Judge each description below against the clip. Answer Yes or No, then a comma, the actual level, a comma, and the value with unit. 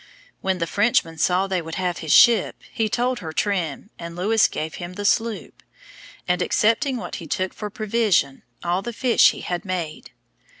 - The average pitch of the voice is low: No, high, 190 Hz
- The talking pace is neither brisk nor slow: Yes, average, 180 wpm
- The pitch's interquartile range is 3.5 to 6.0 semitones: Yes, average, 4.2 semitones